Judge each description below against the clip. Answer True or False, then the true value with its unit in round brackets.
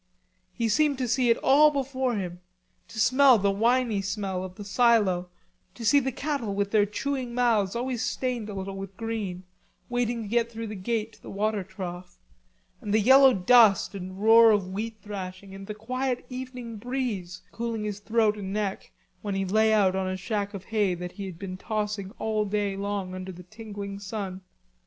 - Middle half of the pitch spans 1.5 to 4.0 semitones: True (3.3 semitones)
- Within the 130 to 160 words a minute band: False (195 wpm)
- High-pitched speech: True (210 Hz)